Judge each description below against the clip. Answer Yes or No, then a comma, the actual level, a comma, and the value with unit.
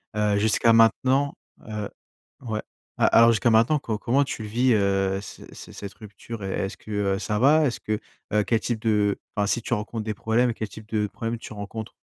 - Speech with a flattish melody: Yes, narrow, 2.1 semitones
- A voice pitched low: Yes, low, 110 Hz